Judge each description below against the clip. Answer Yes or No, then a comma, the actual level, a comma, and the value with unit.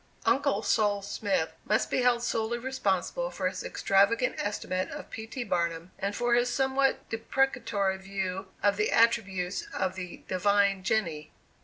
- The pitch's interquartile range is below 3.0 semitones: No, average, 4.0 semitones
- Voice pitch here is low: No, high, 205 Hz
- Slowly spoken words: No, average, 150 wpm